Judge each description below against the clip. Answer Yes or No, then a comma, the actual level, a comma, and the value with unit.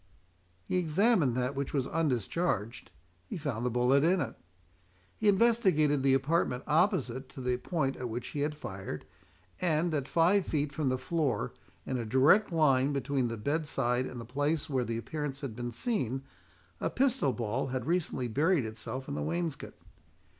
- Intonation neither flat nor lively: Yes, average, 4.6 semitones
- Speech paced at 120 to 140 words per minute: No, average, 170 wpm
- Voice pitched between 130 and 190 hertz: Yes, medium, 140 Hz